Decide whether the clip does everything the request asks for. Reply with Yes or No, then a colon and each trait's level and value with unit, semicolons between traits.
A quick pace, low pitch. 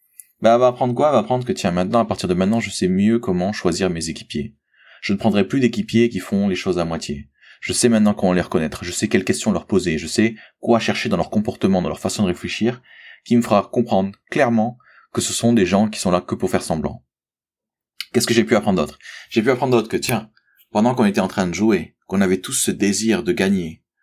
Yes: fast, 250 wpm; low, 110 Hz